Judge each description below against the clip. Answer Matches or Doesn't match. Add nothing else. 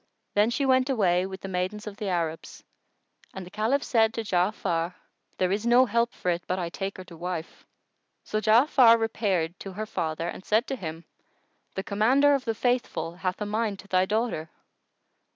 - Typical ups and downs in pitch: Matches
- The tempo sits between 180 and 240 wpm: Matches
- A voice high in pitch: Matches